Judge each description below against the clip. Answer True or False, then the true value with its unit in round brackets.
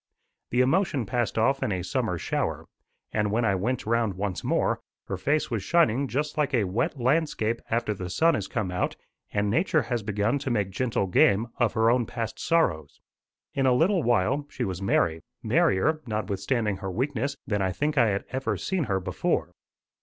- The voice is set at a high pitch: False (115 Hz)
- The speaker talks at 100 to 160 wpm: False (190 wpm)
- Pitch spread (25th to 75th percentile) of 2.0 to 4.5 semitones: False (5.5 semitones)